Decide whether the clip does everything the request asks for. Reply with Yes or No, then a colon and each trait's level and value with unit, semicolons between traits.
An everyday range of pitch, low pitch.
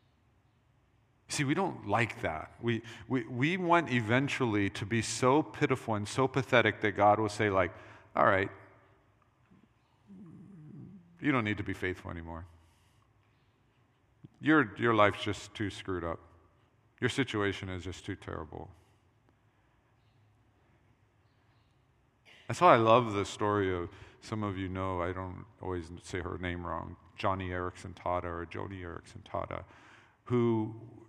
Yes: average, 3.9 semitones; low, 110 Hz